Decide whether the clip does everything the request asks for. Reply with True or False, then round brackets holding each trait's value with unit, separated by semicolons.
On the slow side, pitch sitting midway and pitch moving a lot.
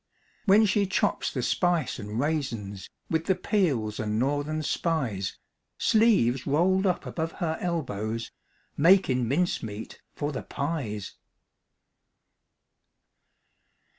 True (105 wpm; 145 Hz; 7.5 semitones)